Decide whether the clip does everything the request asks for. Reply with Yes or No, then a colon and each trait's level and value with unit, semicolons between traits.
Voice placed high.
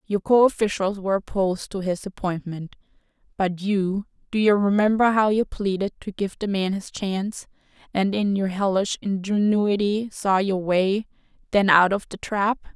Yes: high, 200 Hz